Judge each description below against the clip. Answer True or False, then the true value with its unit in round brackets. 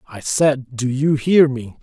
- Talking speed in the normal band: True (195 wpm)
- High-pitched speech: False (135 Hz)